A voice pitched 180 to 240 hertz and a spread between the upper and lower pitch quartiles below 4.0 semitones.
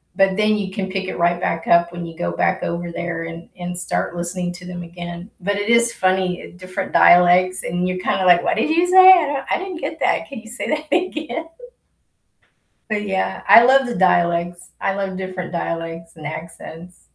Yes: medium, 185 Hz; average, 3.6 semitones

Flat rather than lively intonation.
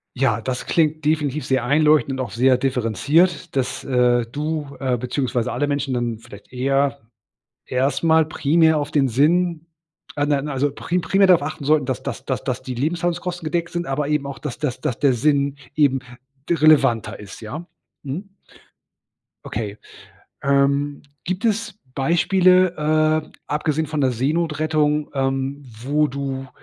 No: average, 3.0 semitones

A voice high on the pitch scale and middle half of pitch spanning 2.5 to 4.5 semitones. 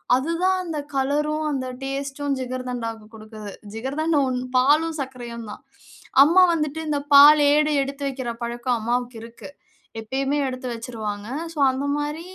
Yes: very high, 265 Hz; average, 3.6 semitones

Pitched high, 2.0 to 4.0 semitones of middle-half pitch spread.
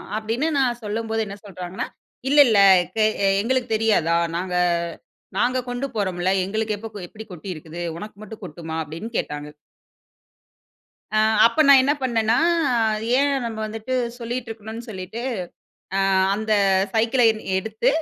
Yes: high, 220 Hz; average, 3.6 semitones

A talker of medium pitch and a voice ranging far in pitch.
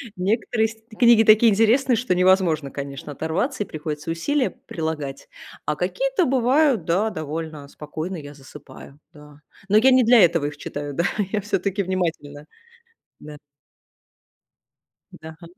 Yes: medium, 180 Hz; wide, 6.9 semitones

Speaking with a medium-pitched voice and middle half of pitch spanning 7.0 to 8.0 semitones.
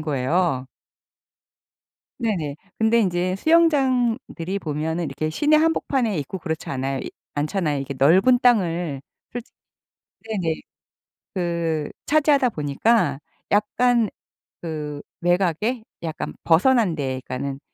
Yes: medium, 175 Hz; wide, 7.5 semitones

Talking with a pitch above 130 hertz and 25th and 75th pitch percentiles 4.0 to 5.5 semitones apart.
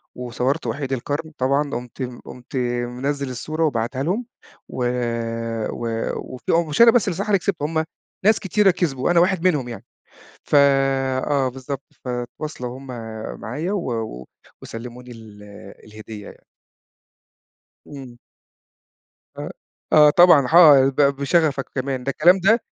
Yes: medium, 140 Hz; average, 4.6 semitones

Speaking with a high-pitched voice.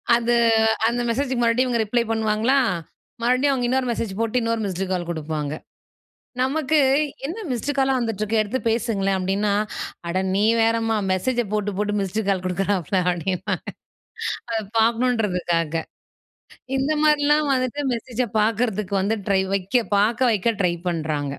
Yes: high, 225 Hz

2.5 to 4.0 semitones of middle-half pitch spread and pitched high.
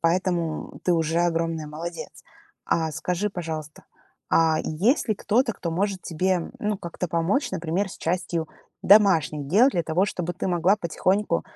No: average, 2.8 semitones; medium, 175 Hz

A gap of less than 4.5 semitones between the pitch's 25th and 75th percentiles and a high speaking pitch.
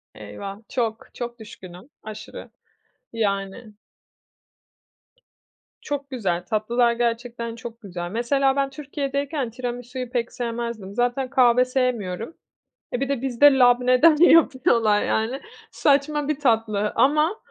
Yes: average, 3.6 semitones; high, 245 Hz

